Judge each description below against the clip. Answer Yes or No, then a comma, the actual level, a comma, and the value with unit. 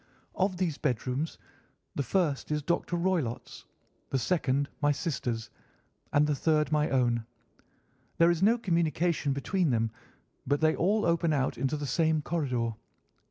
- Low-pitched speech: No, medium, 150 Hz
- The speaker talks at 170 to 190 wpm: No, average, 145 wpm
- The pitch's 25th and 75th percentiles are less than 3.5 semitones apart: No, average, 4.2 semitones